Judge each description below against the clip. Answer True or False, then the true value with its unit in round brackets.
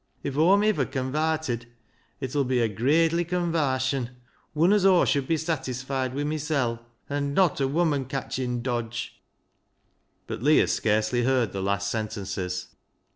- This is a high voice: False (135 Hz)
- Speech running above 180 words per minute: False (145 wpm)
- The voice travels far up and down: False (4.6 semitones)